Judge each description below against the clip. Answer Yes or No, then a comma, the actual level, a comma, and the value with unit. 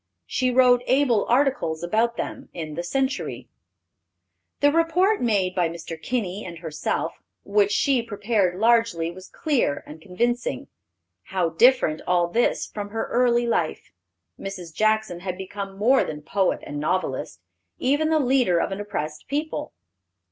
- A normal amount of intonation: No, wide, 6.0 semitones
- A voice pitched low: No, high, 205 Hz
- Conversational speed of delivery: Yes, average, 145 wpm